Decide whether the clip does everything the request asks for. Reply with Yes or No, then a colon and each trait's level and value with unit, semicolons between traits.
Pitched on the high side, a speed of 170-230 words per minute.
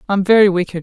Yes: high, 195 Hz; fast, 220 wpm